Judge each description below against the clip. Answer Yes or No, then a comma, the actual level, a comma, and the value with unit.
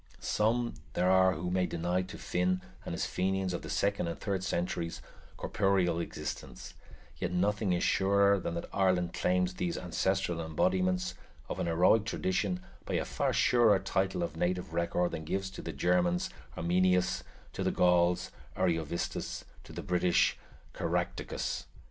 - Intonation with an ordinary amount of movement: No, narrow, 1.8 semitones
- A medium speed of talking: Yes, average, 155 wpm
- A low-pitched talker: Yes, very low, 90 Hz